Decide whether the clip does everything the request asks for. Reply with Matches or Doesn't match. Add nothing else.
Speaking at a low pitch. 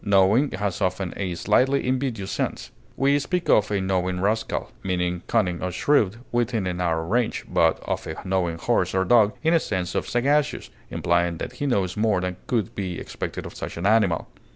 Matches